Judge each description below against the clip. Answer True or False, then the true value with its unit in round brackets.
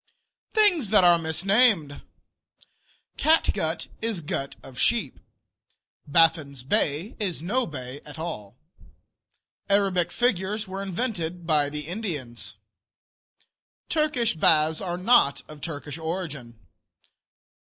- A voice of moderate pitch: True (170 Hz)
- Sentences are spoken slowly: True (100 wpm)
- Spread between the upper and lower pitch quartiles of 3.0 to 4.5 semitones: False (5.6 semitones)